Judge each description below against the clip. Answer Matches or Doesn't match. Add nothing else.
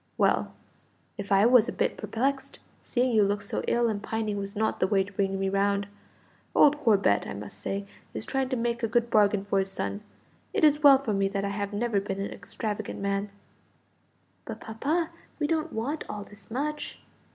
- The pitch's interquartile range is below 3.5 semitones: Doesn't match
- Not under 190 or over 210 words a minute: Matches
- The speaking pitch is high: Matches